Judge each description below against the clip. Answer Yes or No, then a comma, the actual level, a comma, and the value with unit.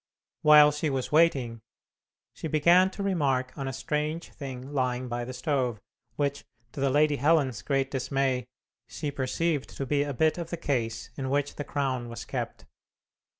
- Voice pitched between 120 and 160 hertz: Yes, medium, 140 Hz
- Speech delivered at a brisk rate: No, average, 170 wpm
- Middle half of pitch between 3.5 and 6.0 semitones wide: No, average, 2.8 semitones